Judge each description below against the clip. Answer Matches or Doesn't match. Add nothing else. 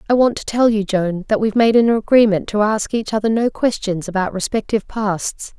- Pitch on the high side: Matches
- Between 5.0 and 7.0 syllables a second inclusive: Matches